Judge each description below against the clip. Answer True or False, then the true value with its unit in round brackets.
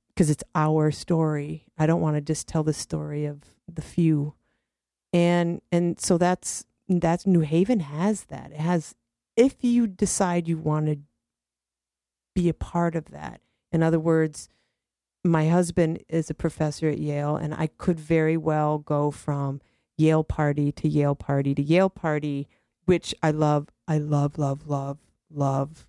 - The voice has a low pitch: False (155 Hz)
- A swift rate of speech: False (160 wpm)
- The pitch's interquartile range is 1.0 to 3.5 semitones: True (2.7 semitones)